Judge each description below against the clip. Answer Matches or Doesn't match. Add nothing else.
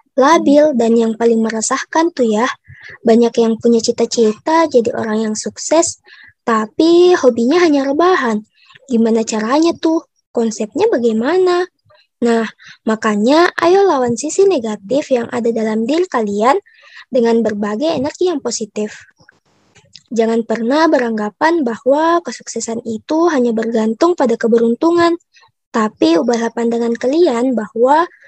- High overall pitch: Matches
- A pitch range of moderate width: Doesn't match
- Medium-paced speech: Matches